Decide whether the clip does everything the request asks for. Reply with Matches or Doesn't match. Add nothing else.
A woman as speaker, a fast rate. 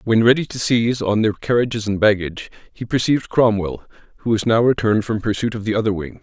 Doesn't match